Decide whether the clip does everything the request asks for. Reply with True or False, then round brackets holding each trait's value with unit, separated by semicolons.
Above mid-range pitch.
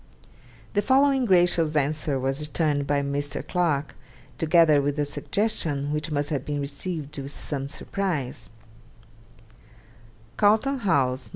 False (150 Hz)